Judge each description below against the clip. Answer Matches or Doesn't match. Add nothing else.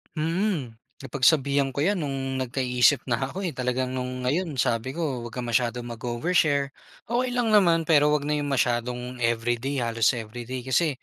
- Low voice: Matches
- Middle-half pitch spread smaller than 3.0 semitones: Doesn't match